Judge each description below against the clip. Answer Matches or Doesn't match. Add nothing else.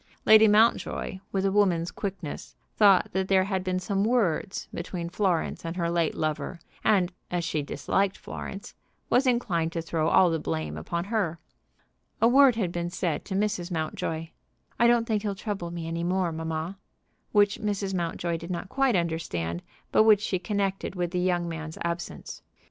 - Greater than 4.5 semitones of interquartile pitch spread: Doesn't match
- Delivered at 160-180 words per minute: Matches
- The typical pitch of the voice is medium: Matches